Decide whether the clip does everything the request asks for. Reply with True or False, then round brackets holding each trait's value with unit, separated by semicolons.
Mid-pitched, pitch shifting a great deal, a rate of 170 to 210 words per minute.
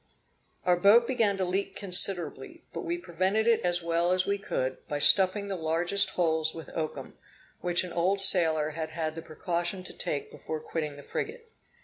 False (175 Hz; 3.4 semitones; 185 wpm)